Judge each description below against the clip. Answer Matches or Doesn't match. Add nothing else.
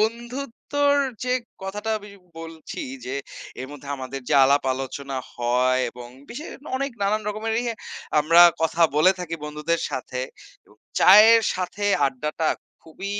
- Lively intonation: Matches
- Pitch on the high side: Doesn't match